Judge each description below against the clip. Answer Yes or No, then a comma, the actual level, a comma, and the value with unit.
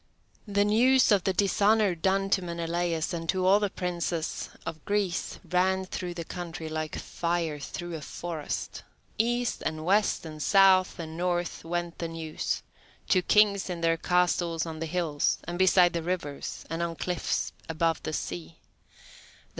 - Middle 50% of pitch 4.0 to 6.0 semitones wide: No, narrow, 2.5 semitones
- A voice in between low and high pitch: Yes, medium, 175 Hz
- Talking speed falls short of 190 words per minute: Yes, average, 160 wpm